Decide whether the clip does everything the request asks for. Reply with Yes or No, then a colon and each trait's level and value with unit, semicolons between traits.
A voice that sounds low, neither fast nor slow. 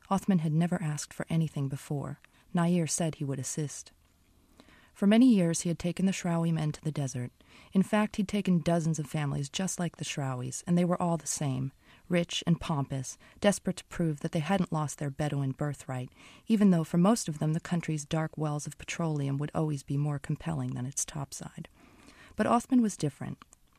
No: medium, 160 Hz; average, 195 wpm